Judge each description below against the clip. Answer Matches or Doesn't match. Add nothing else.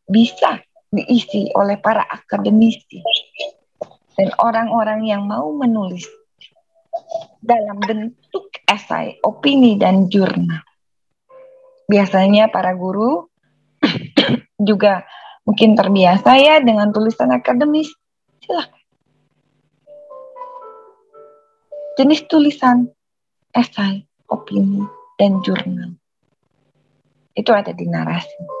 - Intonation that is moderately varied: Doesn't match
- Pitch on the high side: Matches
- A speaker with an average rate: Doesn't match